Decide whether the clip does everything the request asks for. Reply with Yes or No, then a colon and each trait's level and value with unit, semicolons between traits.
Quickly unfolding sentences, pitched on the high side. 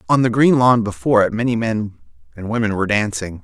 No: fast, 210 wpm; low, 110 Hz